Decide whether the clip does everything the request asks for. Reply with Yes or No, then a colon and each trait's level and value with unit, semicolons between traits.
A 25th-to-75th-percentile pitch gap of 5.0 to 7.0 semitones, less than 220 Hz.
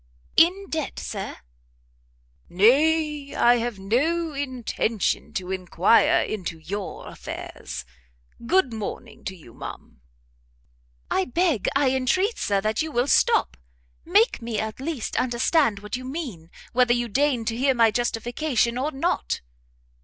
No: average, 5.3 semitones; high, 240 Hz